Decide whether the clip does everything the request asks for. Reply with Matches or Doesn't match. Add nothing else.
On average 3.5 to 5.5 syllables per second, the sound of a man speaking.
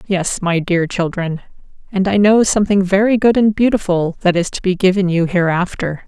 Doesn't match